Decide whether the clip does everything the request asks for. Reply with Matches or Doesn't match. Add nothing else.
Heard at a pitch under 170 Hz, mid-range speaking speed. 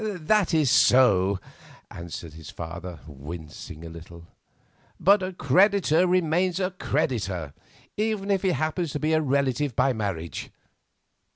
Doesn't match